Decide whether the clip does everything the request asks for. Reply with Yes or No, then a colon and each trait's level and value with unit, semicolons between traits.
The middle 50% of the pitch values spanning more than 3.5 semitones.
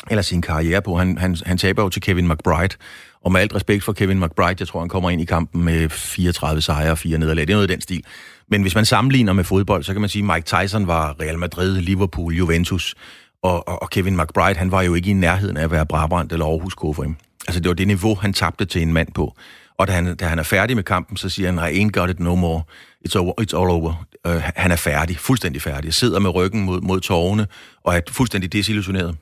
No: average, 2.9 semitones